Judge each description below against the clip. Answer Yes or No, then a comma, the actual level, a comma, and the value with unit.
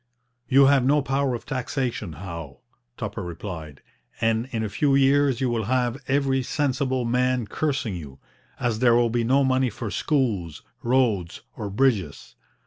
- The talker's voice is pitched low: Yes, low, 125 Hz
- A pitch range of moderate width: Yes, average, 4.1 semitones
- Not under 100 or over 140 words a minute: No, average, 155 wpm